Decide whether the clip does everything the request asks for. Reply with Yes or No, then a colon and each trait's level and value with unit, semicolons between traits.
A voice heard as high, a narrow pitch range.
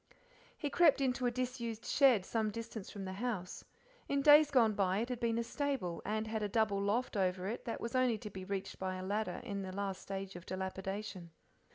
No: high, 215 Hz; average, 4.1 semitones